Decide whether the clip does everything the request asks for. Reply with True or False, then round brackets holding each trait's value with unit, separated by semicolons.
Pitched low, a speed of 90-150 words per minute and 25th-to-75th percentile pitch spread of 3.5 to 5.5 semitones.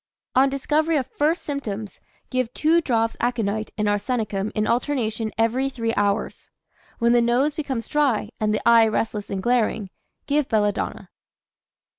False (235 Hz; 145 wpm; 4.0 semitones)